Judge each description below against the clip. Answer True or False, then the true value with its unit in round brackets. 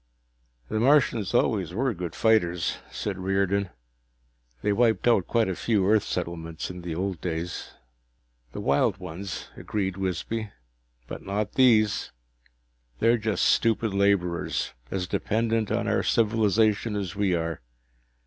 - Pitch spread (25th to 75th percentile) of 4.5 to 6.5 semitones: False (3.7 semitones)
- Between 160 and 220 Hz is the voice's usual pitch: False (100 Hz)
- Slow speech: True (130 wpm)